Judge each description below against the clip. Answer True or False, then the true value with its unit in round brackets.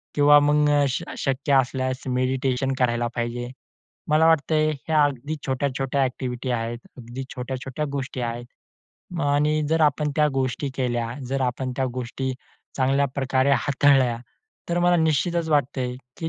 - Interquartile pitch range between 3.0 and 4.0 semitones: False (2.6 semitones)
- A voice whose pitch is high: False (135 Hz)